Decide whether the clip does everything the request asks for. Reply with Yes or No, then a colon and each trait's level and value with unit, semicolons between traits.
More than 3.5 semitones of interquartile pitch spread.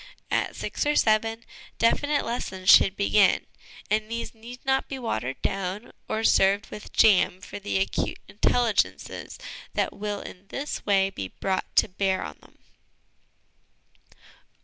No: average, 3.1 semitones